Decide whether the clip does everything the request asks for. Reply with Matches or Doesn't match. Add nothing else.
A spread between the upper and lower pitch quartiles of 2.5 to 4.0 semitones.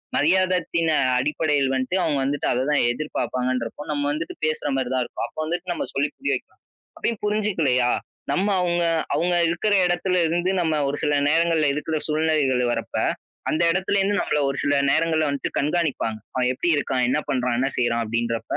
Doesn't match